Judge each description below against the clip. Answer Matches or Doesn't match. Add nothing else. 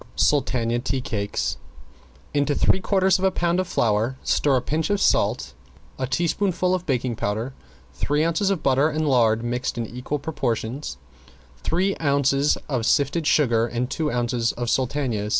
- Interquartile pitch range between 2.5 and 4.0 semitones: Doesn't match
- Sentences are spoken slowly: Doesn't match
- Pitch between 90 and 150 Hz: Matches